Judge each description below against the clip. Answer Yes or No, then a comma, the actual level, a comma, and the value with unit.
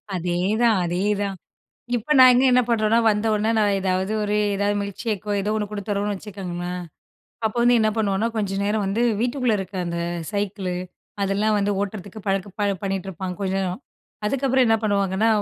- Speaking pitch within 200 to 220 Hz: Yes, high, 205 Hz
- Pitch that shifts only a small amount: Yes, narrow, 2.2 semitones